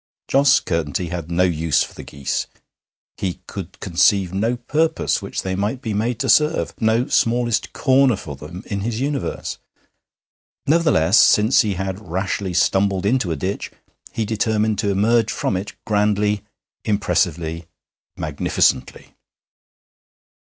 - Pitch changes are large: No, average, 4.6 semitones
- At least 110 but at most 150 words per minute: Yes, slow, 135 wpm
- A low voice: Yes, low, 100 Hz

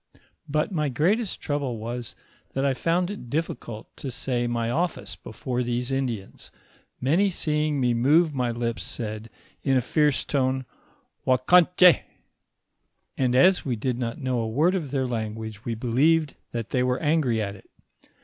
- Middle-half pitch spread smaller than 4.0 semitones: No, average, 4.4 semitones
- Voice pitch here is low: Yes, low, 130 Hz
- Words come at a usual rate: Yes, average, 160 wpm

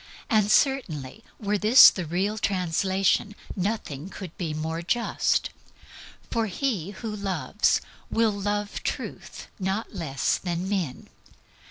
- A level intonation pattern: No, average, 3.6 semitones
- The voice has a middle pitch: No, high, 195 Hz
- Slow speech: Yes, slow, 120 wpm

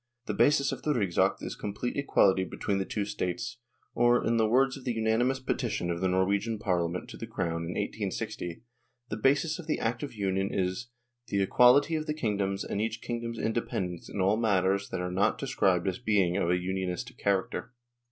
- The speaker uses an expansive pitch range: No, average, 4.4 semitones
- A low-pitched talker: Yes, low, 105 Hz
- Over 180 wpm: Yes, average, 195 wpm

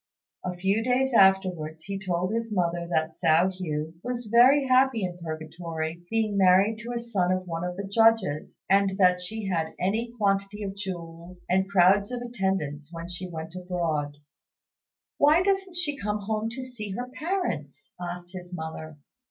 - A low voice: No, high, 190 Hz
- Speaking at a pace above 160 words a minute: Yes, average, 170 wpm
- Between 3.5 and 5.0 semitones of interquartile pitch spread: Yes, average, 4.6 semitones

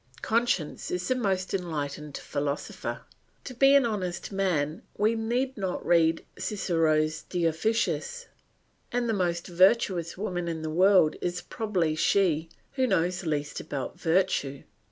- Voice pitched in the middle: Yes, medium, 180 Hz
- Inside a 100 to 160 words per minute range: Yes, slow, 135 wpm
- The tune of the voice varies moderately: Yes, average, 4.9 semitones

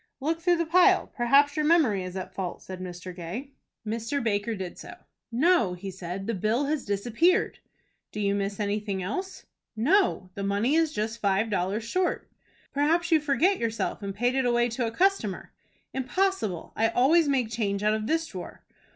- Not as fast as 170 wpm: No, average, 180 wpm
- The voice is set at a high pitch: Yes, high, 230 Hz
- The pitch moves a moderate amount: No, wide, 6.8 semitones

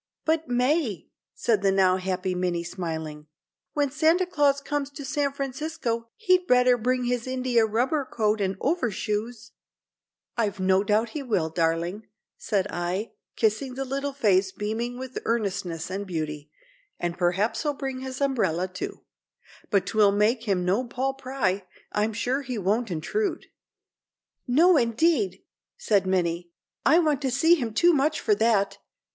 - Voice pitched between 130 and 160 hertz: No, high, 230 Hz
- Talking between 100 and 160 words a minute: Yes, average, 150 wpm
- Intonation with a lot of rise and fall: Yes, wide, 6.2 semitones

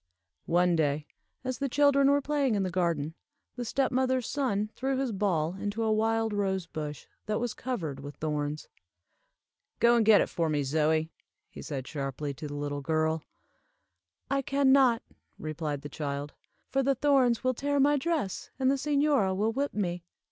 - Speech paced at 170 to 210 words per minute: Yes, average, 175 wpm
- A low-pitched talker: No, high, 205 Hz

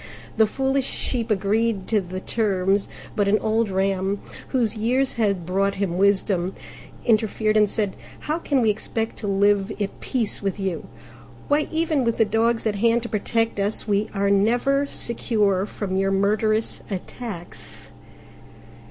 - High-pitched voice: Yes, high, 210 Hz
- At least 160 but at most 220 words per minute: No, average, 150 wpm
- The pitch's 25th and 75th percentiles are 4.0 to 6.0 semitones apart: No, average, 2.7 semitones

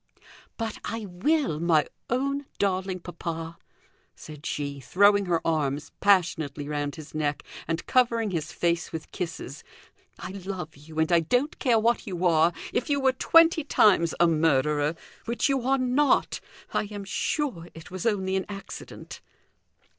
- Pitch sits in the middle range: Yes, medium, 180 Hz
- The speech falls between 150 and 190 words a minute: Yes, average, 155 wpm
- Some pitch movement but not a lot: No, wide, 6.2 semitones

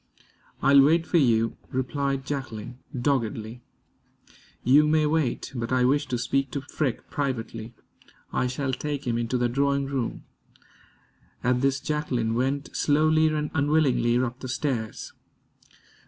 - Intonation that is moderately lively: Yes, average, 3.1 semitones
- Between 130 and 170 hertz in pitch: Yes, low, 135 Hz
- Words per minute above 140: No, slow, 135 wpm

